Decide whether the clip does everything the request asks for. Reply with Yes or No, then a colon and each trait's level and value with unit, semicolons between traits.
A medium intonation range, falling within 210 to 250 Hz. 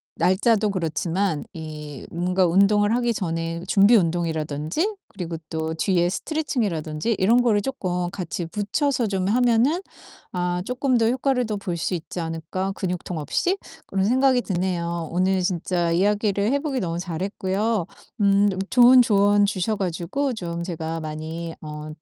No: average, 4.6 semitones; high, 190 Hz